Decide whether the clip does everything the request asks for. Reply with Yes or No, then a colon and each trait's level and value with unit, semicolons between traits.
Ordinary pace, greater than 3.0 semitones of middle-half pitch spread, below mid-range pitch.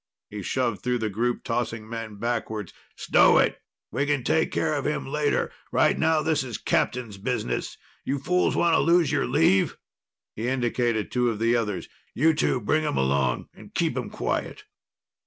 Yes: average, 175 wpm; average, 5.0 semitones; low, 120 Hz